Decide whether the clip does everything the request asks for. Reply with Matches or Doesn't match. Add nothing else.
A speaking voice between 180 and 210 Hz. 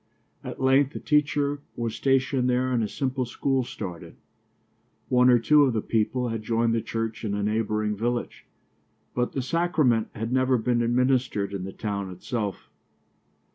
Doesn't match